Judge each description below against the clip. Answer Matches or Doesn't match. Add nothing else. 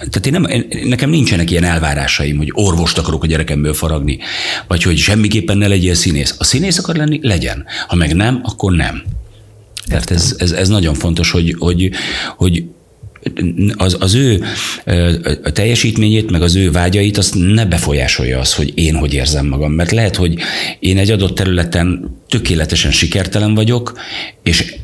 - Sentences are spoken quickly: Matches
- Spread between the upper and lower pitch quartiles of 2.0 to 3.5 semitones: Doesn't match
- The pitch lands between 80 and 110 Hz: Matches